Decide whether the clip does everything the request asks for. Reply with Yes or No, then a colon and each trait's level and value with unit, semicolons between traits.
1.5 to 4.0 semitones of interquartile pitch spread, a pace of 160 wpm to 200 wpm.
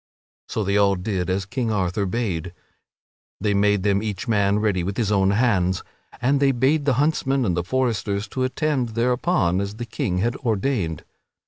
No: average, 4.4 semitones; average, 180 wpm